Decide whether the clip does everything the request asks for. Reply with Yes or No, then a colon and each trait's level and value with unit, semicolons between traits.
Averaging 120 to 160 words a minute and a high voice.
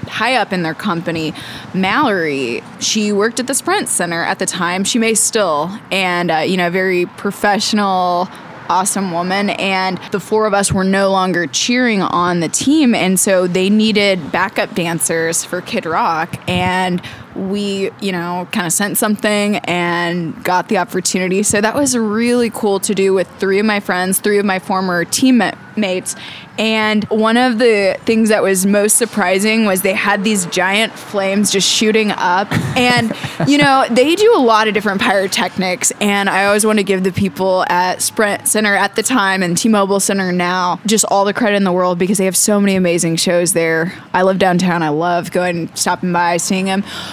No: average, 190 wpm; high, 195 Hz